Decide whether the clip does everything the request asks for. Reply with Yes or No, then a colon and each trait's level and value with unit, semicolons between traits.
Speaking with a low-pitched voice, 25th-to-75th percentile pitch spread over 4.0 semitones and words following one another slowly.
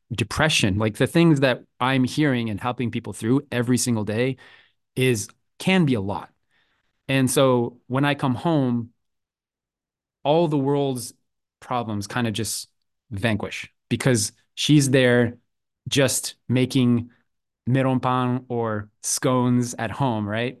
No: low, 125 Hz; narrow, 2.4 semitones; slow, 130 wpm